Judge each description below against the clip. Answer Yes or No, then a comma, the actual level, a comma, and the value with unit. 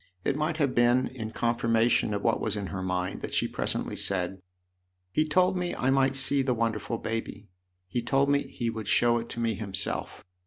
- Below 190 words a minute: No, fast, 205 wpm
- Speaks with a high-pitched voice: No, low, 115 Hz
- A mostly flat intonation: No, average, 4.2 semitones